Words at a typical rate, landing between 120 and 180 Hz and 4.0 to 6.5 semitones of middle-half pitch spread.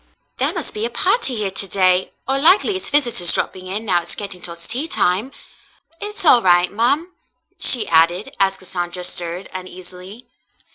No: average, 170 wpm; high, 195 Hz; wide, 5.6 semitones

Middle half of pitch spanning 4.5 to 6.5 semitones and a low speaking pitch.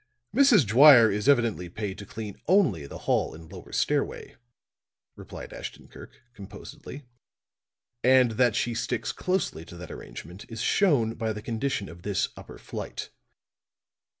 Yes: average, 5.0 semitones; low, 110 Hz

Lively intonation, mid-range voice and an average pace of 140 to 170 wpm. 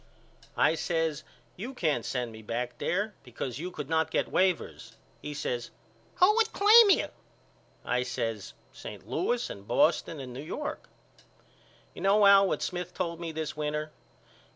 Yes: wide, 7.2 semitones; medium, 160 Hz; average, 155 wpm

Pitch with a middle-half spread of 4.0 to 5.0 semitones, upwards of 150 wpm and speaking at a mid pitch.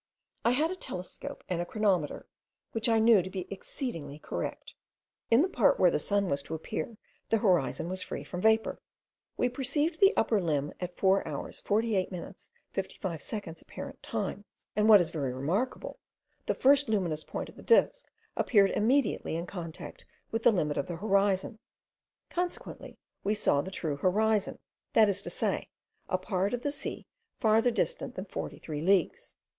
No: average, 4.6 semitones; average, 170 wpm; high, 200 Hz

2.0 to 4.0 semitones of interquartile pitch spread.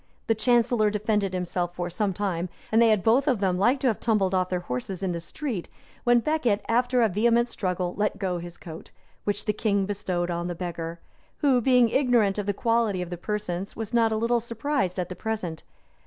No: average, 4.4 semitones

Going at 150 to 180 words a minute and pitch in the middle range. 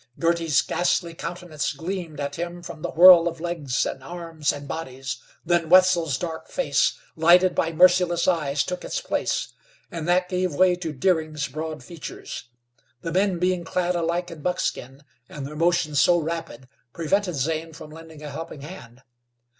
Yes: average, 160 wpm; medium, 165 Hz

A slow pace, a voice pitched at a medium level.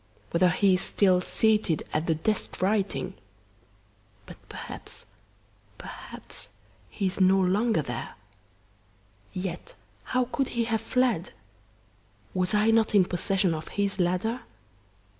No: slow, 120 wpm; high, 195 Hz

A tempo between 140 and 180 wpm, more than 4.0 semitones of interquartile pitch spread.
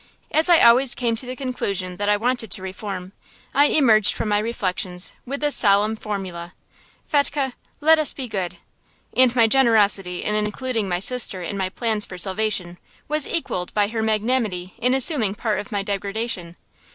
Yes: average, 175 wpm; average, 4.6 semitones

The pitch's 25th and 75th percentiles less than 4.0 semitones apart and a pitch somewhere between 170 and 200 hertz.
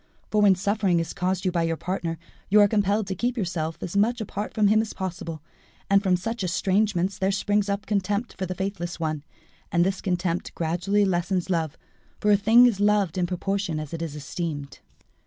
Yes: average, 3.0 semitones; high, 190 Hz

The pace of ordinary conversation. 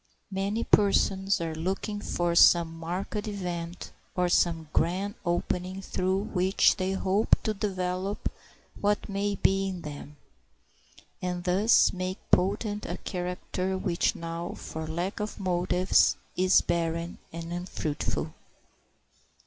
No: slow, 120 wpm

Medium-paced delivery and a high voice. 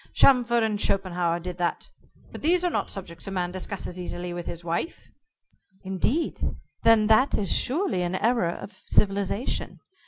Yes: average, 155 wpm; high, 195 Hz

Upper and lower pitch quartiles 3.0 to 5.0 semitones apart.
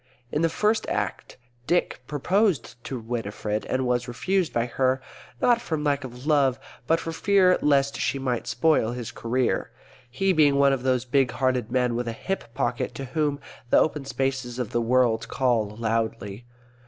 Yes: average, 3.8 semitones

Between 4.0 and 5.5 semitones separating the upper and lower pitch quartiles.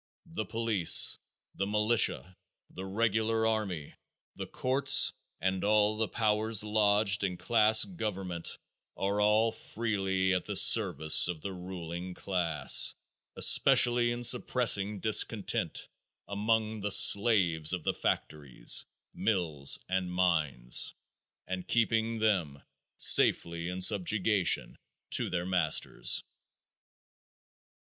No: average, 3.5 semitones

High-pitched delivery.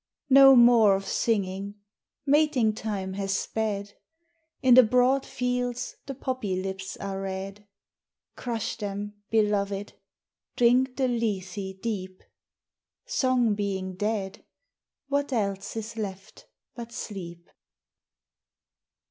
Yes: high, 210 Hz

